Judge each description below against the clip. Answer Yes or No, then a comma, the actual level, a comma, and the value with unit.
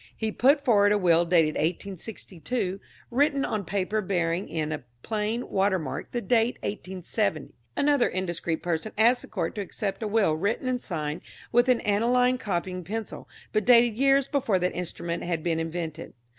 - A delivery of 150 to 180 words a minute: Yes, average, 165 wpm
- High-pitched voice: Yes, high, 200 Hz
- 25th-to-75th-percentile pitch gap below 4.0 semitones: No, wide, 5.4 semitones